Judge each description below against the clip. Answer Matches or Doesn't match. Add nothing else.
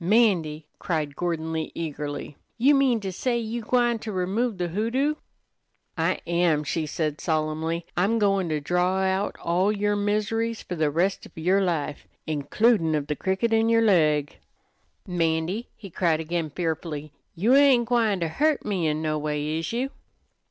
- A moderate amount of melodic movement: Doesn't match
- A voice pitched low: Doesn't match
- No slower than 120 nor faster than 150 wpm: Doesn't match